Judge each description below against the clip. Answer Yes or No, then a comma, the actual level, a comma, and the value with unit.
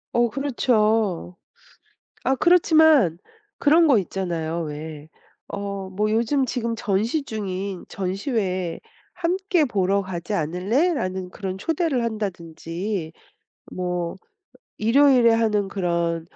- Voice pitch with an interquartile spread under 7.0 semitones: Yes, wide, 5.5 semitones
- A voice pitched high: Yes, high, 200 Hz